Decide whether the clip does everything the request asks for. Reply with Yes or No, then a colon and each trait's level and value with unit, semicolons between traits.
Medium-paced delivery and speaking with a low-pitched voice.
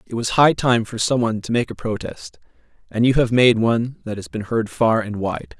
No: fast, 245 wpm; low, 115 Hz